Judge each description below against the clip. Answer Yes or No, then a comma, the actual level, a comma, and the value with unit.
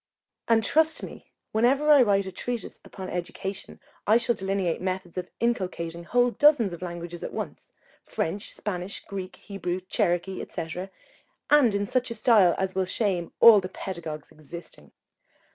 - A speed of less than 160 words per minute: Yes, average, 150 wpm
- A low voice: No, high, 190 Hz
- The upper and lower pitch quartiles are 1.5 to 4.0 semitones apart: No, average, 4.6 semitones